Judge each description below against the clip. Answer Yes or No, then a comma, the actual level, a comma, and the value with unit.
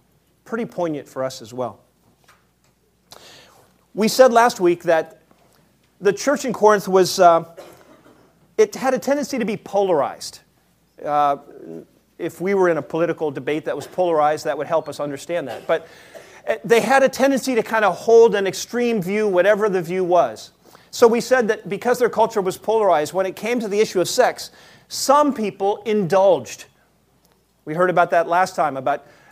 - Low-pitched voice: No, high, 190 Hz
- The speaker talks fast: No, average, 170 wpm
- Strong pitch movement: Yes, wide, 5.7 semitones